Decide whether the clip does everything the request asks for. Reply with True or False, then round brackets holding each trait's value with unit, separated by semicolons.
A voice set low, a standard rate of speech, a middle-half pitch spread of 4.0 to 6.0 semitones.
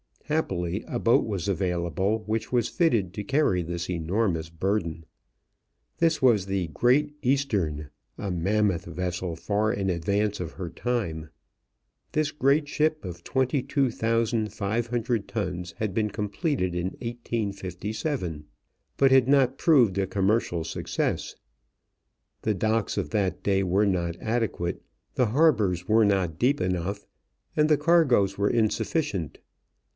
False (105 Hz; 130 wpm; 5.2 semitones)